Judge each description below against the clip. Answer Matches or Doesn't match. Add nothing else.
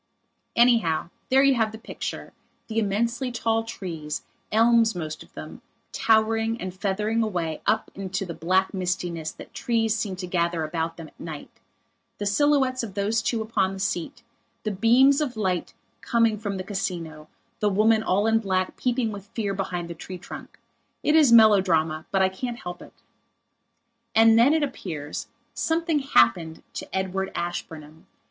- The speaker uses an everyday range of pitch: Matches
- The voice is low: Doesn't match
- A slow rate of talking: Doesn't match